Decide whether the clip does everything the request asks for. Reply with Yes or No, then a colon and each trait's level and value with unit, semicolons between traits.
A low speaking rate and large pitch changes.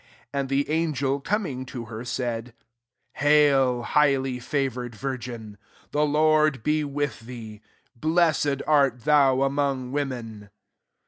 No: slow, 130 wpm; average, 3.0 semitones